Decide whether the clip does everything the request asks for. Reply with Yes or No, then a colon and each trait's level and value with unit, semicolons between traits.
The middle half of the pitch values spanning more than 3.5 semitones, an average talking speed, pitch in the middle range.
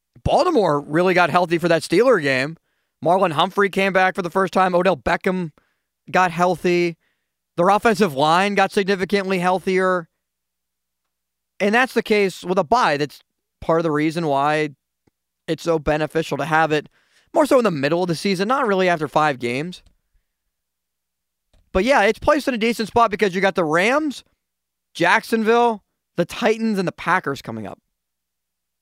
Yes: average, 5.1 semitones; average, 165 wpm; medium, 180 Hz